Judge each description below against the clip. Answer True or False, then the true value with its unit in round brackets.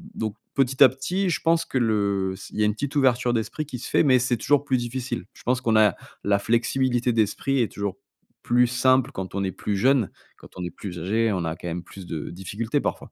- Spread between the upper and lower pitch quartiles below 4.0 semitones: False (4.6 semitones)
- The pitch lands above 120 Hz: False (115 Hz)